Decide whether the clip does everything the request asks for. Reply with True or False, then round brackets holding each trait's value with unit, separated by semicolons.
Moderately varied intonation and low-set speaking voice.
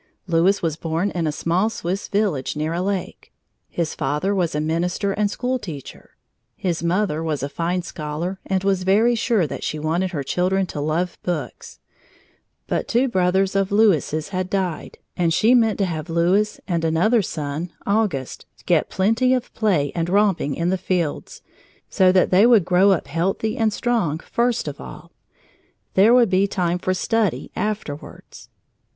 False (3.7 semitones; 185 Hz)